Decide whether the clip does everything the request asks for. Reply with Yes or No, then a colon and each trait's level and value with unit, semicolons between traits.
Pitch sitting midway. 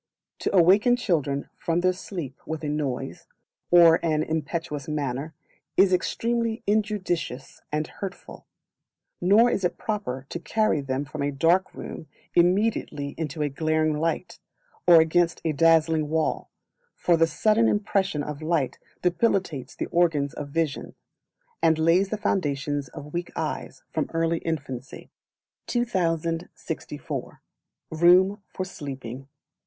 Yes: medium, 165 Hz